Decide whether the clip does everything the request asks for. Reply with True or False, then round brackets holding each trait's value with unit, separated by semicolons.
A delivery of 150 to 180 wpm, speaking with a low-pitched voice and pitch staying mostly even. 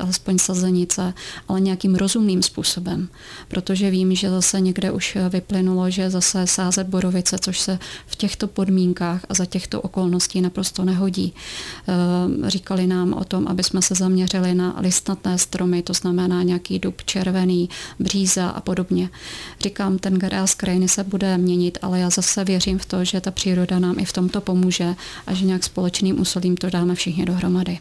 False (170 wpm; 185 Hz; 0.9 semitones)